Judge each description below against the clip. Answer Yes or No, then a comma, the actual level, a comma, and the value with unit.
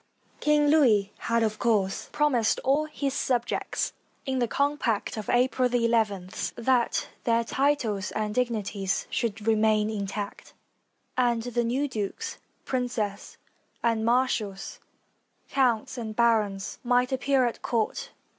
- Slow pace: Yes, slow, 120 wpm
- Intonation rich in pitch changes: No, average, 3.1 semitones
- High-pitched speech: Yes, high, 235 Hz